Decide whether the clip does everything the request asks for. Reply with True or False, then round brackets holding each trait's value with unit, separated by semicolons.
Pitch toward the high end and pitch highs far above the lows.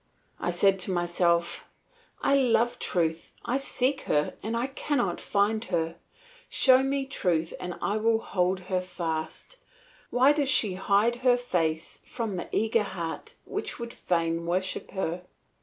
True (195 Hz; 5.8 semitones)